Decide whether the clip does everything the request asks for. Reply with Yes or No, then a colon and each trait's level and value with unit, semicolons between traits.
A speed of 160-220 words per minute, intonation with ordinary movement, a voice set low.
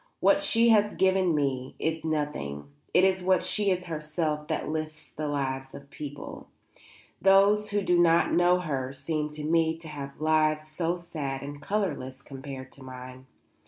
No: average, 170 wpm; average, 4.2 semitones; medium, 155 Hz